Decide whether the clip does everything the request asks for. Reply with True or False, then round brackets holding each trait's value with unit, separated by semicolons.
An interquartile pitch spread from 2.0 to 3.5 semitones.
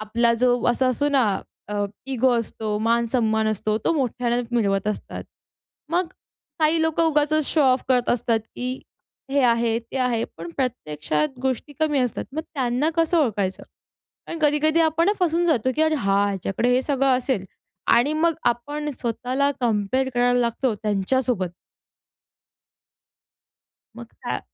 False (4.5 semitones)